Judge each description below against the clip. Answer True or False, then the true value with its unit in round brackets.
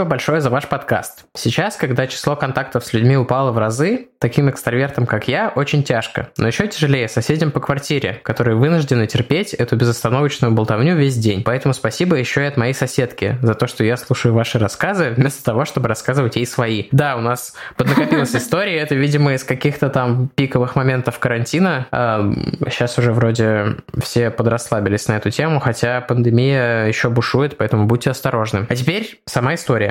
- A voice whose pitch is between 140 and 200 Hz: False (125 Hz)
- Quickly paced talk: True (170 wpm)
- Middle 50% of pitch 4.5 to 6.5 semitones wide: False (3.4 semitones)